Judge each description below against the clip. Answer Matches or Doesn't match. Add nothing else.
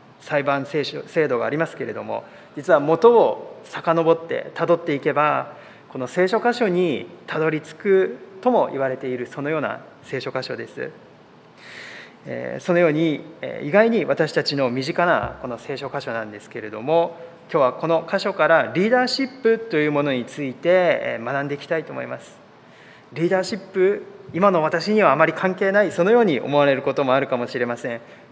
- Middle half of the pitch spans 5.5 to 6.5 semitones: Matches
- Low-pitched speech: Doesn't match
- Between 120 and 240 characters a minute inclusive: Doesn't match